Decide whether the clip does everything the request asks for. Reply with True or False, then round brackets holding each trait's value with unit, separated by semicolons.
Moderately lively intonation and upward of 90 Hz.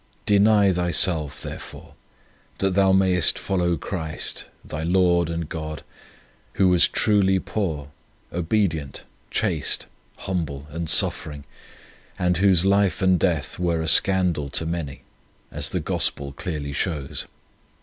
False (3.5 semitones; 85 Hz)